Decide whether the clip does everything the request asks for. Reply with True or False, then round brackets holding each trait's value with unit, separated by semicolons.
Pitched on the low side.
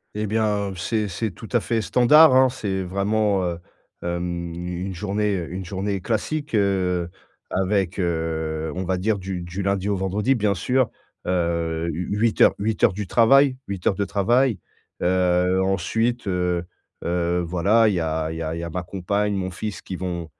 True (95 Hz)